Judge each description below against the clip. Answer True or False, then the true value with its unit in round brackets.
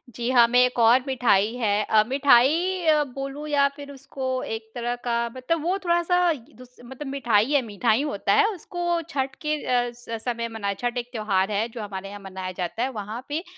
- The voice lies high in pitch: True (245 Hz)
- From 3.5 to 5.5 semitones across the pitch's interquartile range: True (4.4 semitones)